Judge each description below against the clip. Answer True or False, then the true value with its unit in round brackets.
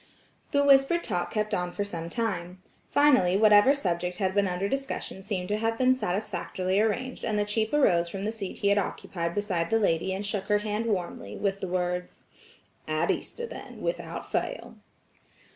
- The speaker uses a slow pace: False (180 wpm)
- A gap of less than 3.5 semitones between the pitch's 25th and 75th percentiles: False (3.8 semitones)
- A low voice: False (200 Hz)